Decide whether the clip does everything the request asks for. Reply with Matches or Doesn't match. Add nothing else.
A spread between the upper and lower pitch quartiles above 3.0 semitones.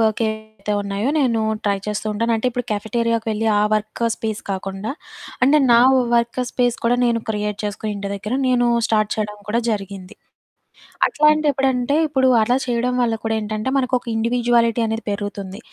Doesn't match